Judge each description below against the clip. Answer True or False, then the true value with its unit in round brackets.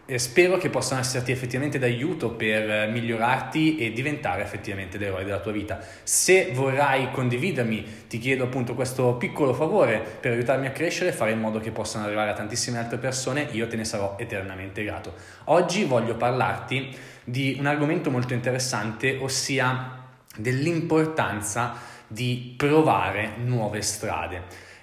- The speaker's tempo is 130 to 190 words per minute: True (145 wpm)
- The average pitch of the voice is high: False (125 Hz)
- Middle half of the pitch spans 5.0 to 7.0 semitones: False (3.3 semitones)